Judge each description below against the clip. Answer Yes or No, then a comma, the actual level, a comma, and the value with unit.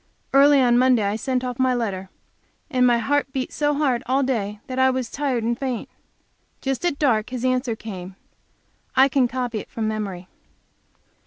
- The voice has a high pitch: Yes, very high, 250 Hz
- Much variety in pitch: No, average, 3.0 semitones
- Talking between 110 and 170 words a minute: No, average, 180 wpm